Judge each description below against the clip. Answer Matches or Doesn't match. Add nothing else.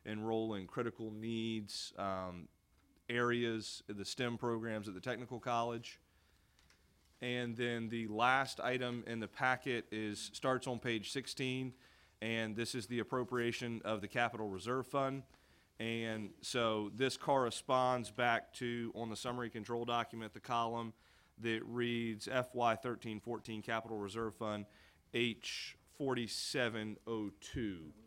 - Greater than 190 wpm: Doesn't match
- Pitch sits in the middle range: Doesn't match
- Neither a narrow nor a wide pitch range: Doesn't match